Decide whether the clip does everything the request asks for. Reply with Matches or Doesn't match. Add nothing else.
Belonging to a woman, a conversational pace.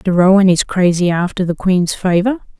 Matches